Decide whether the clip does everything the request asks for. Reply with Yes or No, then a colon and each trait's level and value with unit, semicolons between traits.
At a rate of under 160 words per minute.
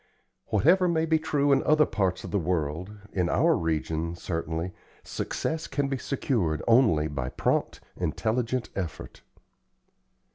Yes: slow, 135 wpm